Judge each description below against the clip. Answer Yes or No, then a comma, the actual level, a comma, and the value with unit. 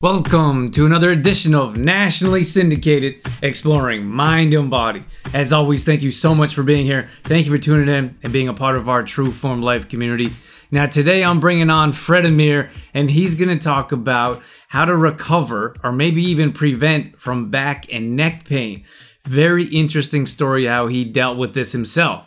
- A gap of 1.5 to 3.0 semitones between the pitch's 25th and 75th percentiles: No, average, 3.7 semitones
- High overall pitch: No, medium, 145 Hz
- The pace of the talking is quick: No, average, 185 wpm